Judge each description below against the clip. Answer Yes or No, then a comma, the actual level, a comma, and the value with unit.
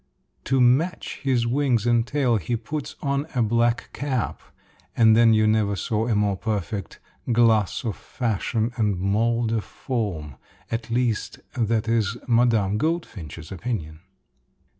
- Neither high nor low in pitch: No, low, 115 Hz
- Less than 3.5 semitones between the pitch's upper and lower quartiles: Yes, narrow, 2.6 semitones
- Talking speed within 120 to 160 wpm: Yes, average, 140 wpm